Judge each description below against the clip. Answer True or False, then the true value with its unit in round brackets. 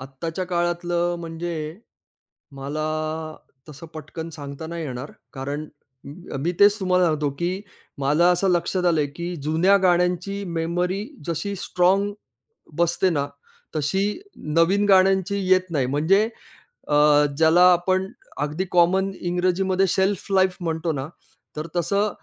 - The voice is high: False (175 Hz)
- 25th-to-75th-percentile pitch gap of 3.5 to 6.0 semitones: False (3.1 semitones)